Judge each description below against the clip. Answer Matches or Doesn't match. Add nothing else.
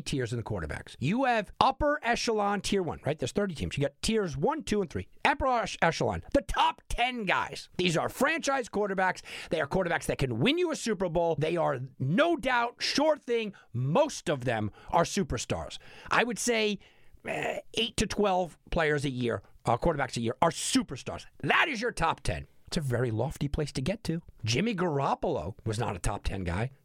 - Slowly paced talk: Doesn't match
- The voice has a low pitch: Doesn't match